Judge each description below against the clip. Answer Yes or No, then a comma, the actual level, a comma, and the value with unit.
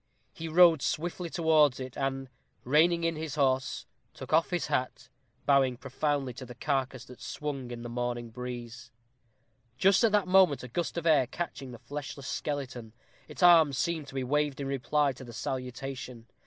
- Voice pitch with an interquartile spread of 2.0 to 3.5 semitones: No, average, 3.9 semitones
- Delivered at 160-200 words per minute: Yes, average, 175 wpm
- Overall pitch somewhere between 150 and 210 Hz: No, medium, 140 Hz